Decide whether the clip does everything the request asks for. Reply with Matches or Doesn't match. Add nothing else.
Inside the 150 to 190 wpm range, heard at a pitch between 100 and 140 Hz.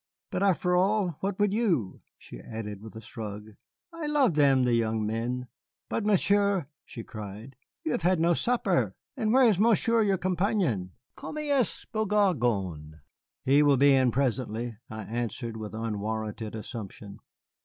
Matches